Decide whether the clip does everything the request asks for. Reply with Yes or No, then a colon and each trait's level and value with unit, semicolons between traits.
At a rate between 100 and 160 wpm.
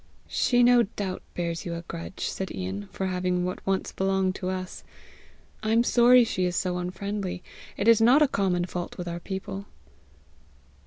No: average, 175 wpm